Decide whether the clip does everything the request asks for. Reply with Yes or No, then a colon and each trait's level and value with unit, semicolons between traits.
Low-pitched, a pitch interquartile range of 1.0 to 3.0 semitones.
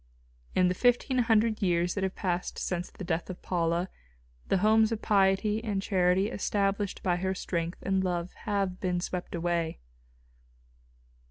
No: high, 190 Hz; average, 2.7 semitones